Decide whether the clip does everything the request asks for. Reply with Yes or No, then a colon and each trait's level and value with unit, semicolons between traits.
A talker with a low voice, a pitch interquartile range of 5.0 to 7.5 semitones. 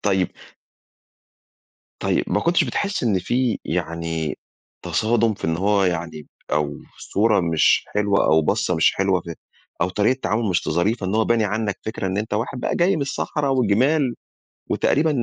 Yes: low, 105 Hz; wide, 5.4 semitones